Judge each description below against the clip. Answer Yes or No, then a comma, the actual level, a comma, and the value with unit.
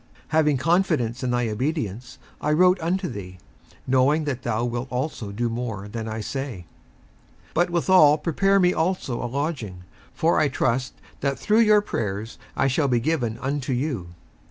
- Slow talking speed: No, average, 170 wpm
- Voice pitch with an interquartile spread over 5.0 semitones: Yes, wide, 5.4 semitones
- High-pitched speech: No, low, 130 Hz